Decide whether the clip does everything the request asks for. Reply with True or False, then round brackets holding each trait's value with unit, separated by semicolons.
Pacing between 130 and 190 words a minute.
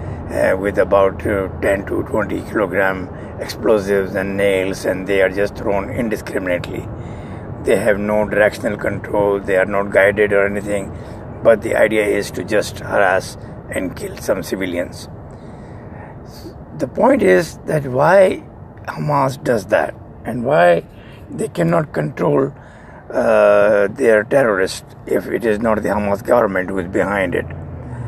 True (140 wpm)